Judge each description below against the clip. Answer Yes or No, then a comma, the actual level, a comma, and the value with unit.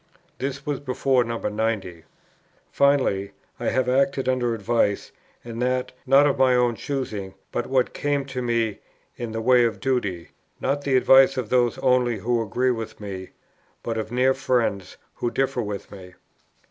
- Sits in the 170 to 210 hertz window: No, low, 120 Hz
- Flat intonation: No, average, 3.1 semitones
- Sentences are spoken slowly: No, average, 165 wpm